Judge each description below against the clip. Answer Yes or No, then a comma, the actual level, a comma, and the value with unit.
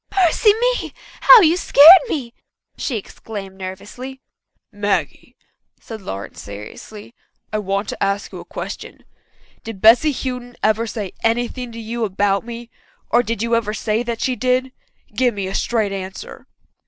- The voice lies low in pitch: No, high, 230 Hz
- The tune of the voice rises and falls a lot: No, average, 3.7 semitones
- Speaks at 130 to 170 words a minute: Yes, average, 155 wpm